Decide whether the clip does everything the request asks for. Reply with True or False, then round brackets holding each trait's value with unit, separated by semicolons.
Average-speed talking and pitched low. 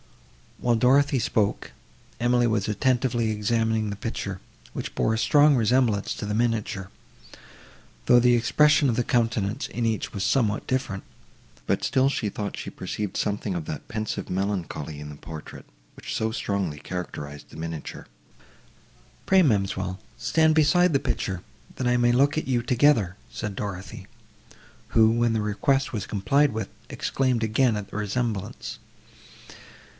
True (150 wpm; 110 Hz)